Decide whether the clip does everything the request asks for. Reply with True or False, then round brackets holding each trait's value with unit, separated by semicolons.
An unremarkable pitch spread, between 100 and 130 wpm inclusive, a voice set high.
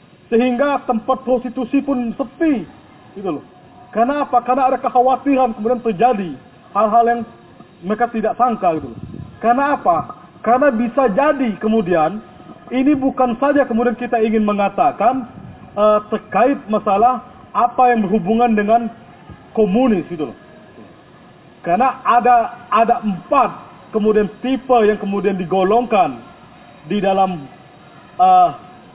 True (3.2 semitones; 115 wpm; 240 Hz)